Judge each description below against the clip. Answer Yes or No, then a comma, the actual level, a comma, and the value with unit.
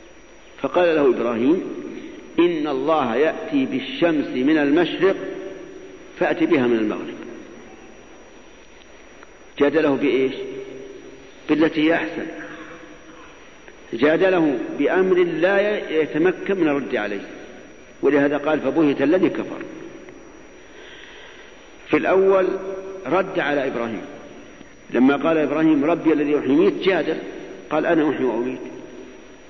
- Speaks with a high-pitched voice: Yes, high, 195 Hz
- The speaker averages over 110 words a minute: No, average, 90 wpm